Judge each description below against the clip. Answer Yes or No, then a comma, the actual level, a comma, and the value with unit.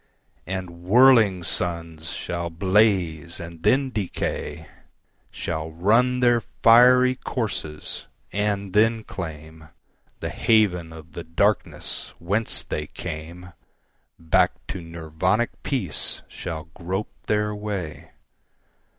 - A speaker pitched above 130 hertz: No, very low, 90 Hz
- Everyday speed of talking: No, slow, 90 wpm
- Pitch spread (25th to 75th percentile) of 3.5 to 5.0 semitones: Yes, average, 4.6 semitones